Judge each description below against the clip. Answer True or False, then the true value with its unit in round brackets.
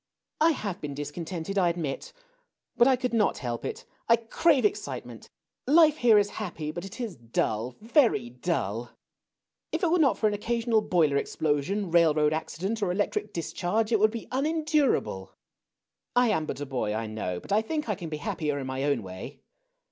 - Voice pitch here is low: False (180 Hz)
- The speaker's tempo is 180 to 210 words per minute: True (195 wpm)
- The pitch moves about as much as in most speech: False (8.2 semitones)